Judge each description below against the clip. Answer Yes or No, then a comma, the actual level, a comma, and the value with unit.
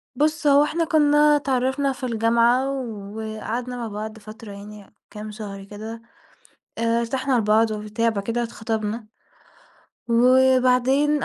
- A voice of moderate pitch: No, high, 230 Hz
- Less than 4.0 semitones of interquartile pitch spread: Yes, average, 3.4 semitones